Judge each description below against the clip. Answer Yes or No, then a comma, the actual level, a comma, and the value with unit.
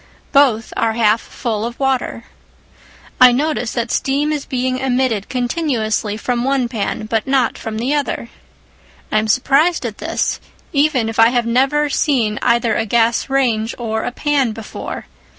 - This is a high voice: Yes, high, 245 Hz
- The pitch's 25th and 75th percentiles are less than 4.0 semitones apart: Yes, average, 3.3 semitones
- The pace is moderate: Yes, average, 165 wpm